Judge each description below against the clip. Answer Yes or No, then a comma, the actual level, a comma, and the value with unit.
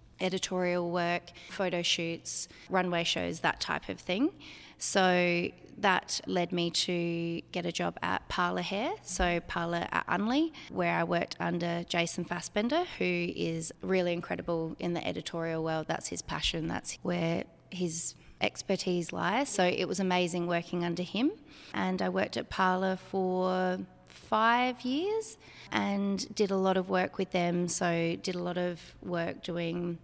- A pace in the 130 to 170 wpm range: Yes, average, 155 wpm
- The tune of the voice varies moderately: No, narrow, 1.7 semitones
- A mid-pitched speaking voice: Yes, medium, 180 Hz